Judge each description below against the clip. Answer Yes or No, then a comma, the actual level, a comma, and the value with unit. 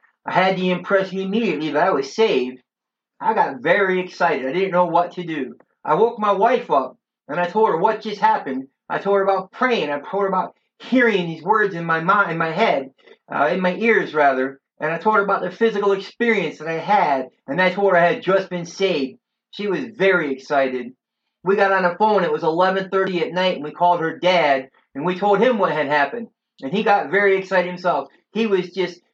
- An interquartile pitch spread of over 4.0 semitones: No, average, 3.3 semitones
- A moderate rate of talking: No, fast, 225 wpm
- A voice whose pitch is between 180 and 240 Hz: Yes, high, 190 Hz